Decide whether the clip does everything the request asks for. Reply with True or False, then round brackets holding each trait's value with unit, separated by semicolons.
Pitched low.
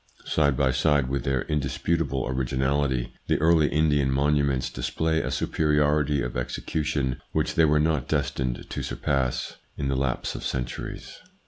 True (70 Hz)